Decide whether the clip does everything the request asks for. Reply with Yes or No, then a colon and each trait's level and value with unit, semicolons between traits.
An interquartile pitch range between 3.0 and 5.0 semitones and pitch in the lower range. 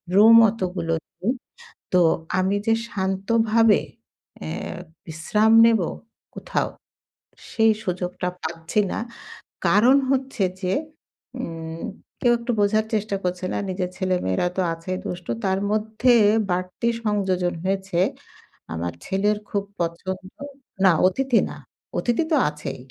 No: average, 3.4 semitones; high, 190 Hz